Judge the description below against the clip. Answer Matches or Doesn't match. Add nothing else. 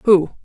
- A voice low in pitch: Doesn't match